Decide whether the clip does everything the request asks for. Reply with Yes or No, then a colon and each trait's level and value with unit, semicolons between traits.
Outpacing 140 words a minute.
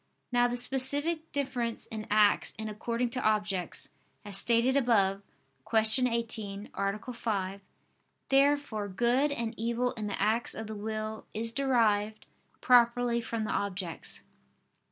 No: slow, 135 wpm